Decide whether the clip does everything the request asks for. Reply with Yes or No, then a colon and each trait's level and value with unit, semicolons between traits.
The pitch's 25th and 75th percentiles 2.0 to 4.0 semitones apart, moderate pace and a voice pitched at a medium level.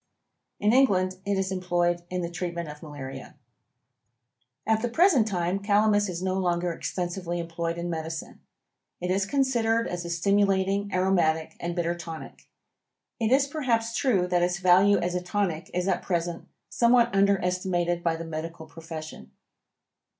Yes: average, 2.9 semitones; average, 150 wpm; medium, 180 Hz